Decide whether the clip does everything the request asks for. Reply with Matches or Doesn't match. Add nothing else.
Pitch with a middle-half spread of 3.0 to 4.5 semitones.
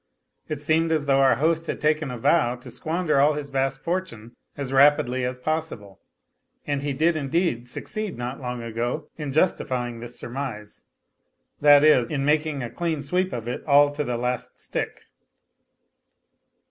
Matches